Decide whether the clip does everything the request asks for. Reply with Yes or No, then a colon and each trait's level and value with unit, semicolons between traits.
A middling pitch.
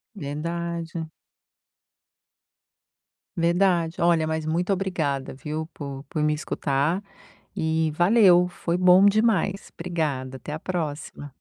Yes: medium, 165 Hz